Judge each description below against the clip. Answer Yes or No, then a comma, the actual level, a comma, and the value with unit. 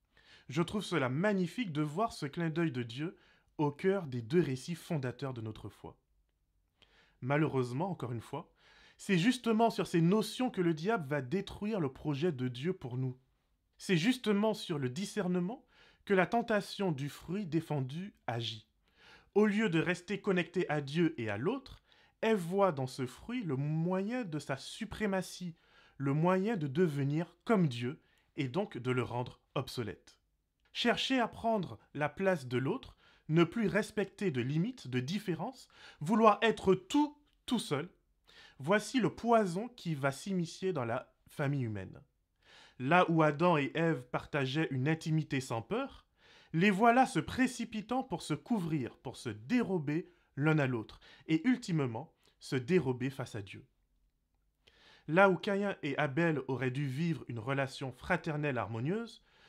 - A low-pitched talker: No, medium, 165 Hz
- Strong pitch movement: Yes, wide, 6.6 semitones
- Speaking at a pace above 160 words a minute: No, average, 155 wpm